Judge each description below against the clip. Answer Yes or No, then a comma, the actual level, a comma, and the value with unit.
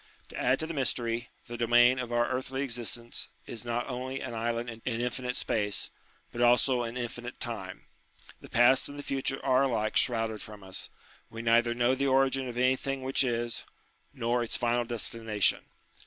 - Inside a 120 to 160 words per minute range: No, average, 175 wpm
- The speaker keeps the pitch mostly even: Yes, narrow, 1.9 semitones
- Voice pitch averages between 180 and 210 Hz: No, low, 120 Hz